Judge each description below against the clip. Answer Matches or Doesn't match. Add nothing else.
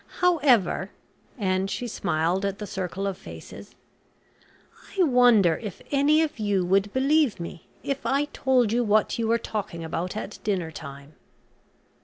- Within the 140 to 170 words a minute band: Matches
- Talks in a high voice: Matches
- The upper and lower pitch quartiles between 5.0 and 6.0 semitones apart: Matches